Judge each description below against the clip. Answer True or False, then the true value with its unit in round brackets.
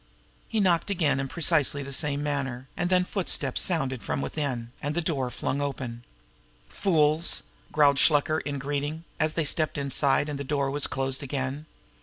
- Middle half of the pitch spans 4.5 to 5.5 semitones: False (2.5 semitones)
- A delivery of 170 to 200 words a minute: True (180 wpm)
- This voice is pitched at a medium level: True (145 Hz)